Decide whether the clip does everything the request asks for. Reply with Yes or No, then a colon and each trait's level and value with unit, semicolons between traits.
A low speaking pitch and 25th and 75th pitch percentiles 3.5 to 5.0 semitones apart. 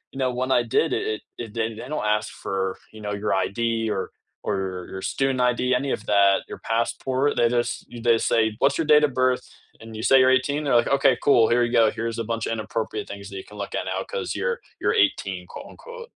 Yes: low, 120 Hz; average, 3.8 semitones